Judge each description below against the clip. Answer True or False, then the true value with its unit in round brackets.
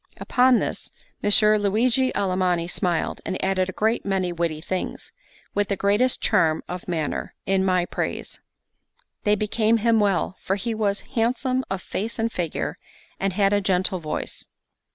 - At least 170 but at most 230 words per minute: False (155 wpm)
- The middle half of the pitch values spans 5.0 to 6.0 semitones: False (3.1 semitones)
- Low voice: False (200 Hz)